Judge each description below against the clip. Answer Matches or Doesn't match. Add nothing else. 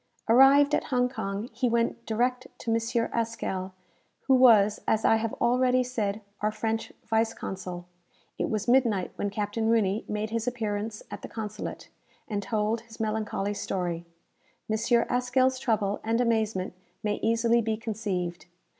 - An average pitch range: Doesn't match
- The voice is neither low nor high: Doesn't match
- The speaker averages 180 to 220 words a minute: Doesn't match